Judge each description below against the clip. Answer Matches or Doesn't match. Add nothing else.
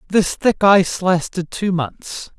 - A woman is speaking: Doesn't match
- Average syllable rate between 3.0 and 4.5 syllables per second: Matches